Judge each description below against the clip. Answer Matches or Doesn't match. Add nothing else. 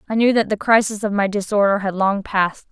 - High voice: Matches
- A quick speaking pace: Matches